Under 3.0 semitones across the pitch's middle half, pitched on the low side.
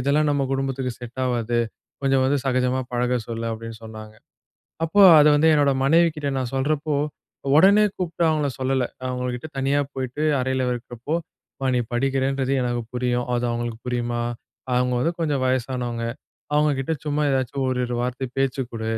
Yes: narrow, 2.6 semitones; low, 130 Hz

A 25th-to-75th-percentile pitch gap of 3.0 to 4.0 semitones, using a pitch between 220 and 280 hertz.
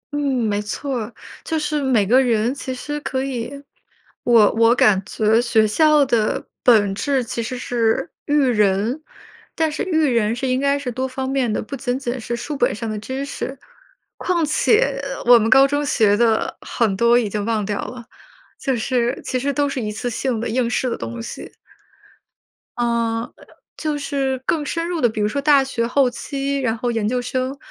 Yes: average, 3.5 semitones; high, 245 Hz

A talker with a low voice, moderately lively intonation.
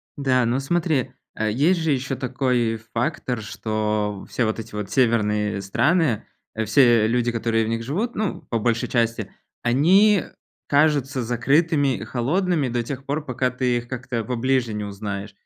Yes: low, 125 Hz; average, 3.8 semitones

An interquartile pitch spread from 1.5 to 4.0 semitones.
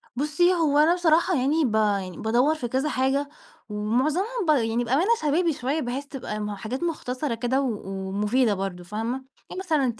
No: wide, 5.6 semitones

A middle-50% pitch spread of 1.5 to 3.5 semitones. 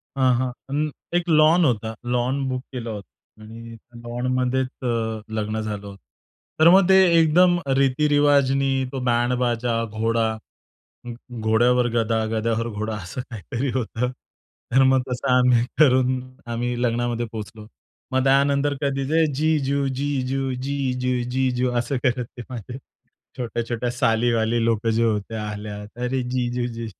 Yes: average, 2.7 semitones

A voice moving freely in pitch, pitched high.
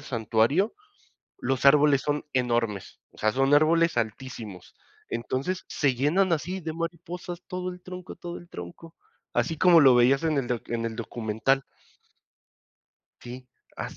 No: wide, 6.0 semitones; medium, 140 Hz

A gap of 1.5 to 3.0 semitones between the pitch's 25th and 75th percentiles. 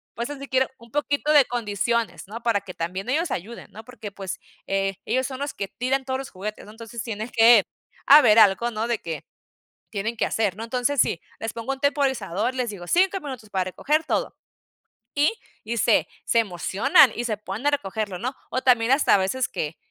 No: average, 4.5 semitones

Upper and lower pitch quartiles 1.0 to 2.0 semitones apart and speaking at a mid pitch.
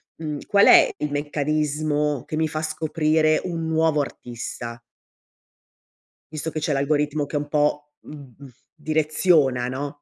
Yes: narrow, 1.3 semitones; medium, 150 Hz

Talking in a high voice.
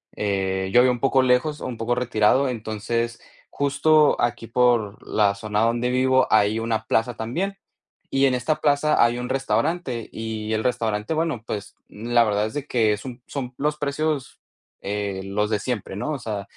No: low, 120 Hz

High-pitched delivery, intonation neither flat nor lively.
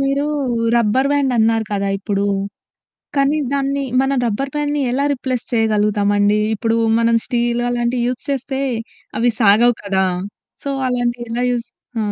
Yes: high, 240 Hz; average, 3.6 semitones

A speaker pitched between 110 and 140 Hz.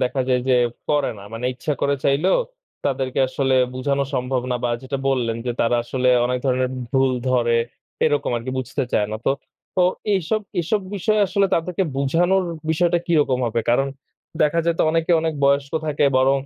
Yes: low, 135 Hz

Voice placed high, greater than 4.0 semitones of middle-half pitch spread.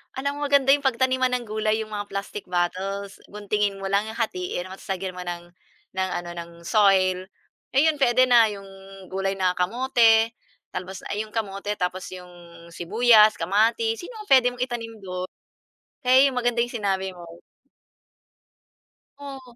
Yes: high, 210 Hz; average, 4.5 semitones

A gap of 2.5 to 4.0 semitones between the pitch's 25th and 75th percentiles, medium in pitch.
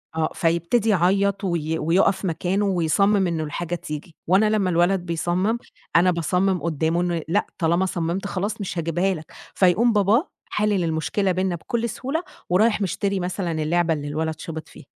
Yes: average, 3.2 semitones; medium, 180 Hz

